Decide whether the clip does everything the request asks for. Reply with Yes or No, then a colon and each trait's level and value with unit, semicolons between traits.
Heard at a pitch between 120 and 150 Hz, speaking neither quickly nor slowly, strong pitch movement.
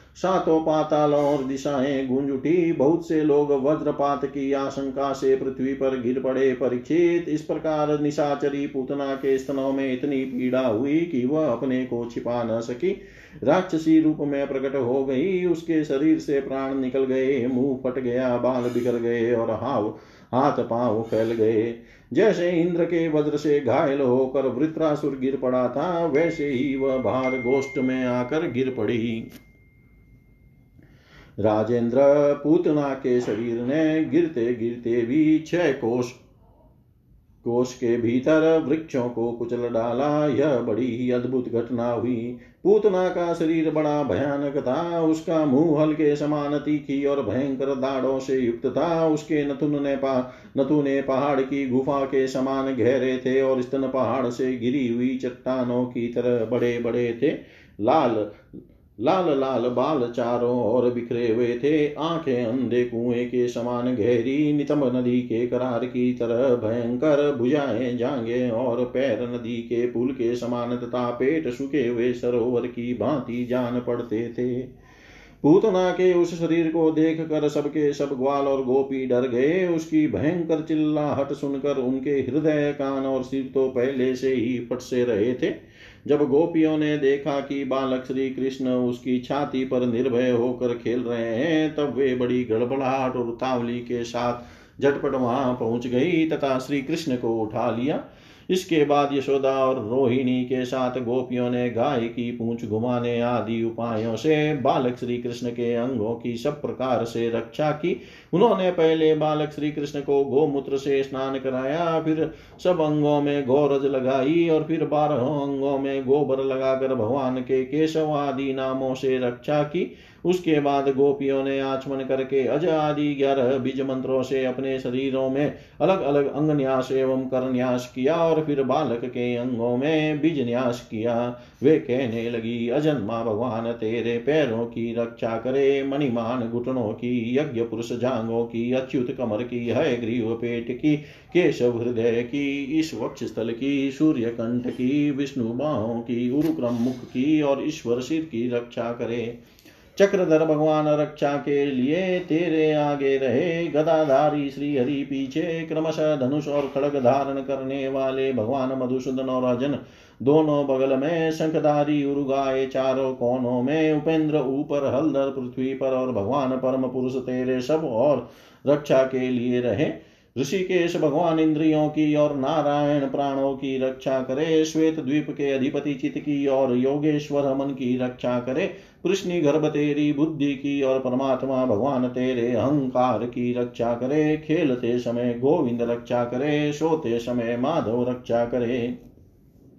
No: low, 135 Hz; average, 150 wpm; average, 3.1 semitones